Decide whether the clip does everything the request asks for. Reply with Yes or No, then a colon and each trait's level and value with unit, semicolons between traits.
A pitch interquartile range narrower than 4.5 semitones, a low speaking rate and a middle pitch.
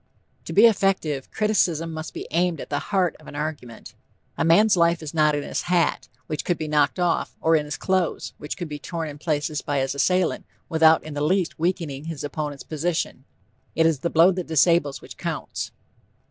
No: average, 2.9 semitones; average, 200 wpm; medium, 160 Hz